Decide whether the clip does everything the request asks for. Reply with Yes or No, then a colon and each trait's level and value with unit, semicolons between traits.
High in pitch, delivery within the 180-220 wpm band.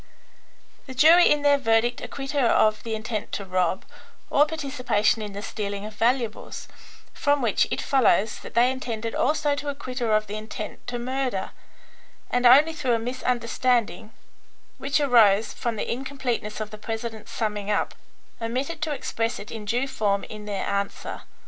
No: high, 235 Hz; average, 170 wpm